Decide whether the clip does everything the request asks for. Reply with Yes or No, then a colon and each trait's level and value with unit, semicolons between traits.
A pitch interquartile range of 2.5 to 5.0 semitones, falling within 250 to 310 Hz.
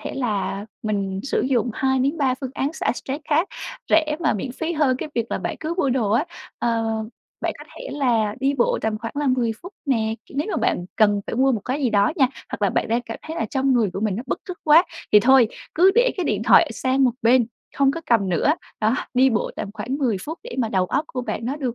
Yes: average, 4.5 semitones; very high, 255 Hz